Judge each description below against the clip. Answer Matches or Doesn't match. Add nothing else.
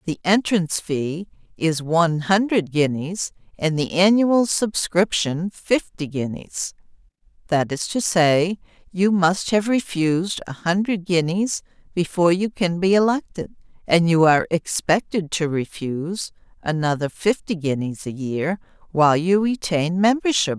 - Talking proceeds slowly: Matches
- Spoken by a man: Doesn't match